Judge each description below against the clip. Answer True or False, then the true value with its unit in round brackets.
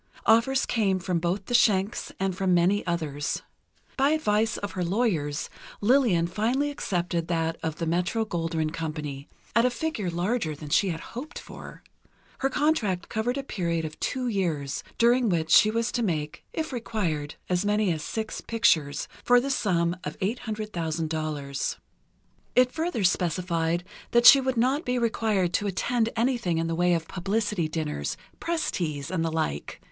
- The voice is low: False (185 Hz)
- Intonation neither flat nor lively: False (6.0 semitones)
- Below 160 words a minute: False (165 wpm)